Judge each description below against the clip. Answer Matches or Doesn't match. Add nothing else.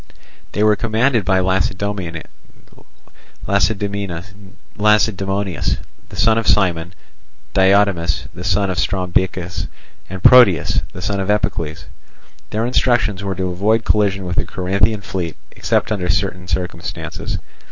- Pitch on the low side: Matches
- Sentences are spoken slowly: Matches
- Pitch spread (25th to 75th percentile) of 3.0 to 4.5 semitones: Doesn't match